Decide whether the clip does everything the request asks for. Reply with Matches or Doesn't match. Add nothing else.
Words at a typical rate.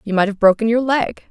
Doesn't match